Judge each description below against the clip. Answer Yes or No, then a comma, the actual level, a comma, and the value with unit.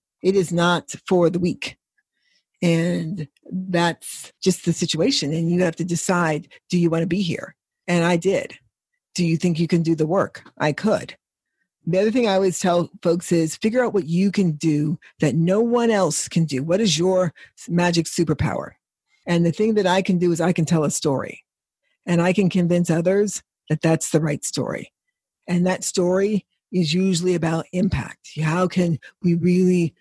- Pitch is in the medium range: Yes, medium, 175 Hz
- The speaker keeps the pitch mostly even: Yes, narrow, 2.1 semitones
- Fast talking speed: No, average, 190 wpm